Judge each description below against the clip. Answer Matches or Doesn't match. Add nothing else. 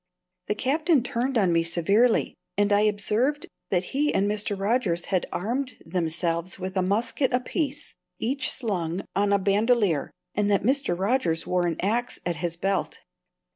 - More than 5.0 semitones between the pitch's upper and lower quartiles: Matches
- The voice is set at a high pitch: Matches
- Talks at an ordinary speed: Matches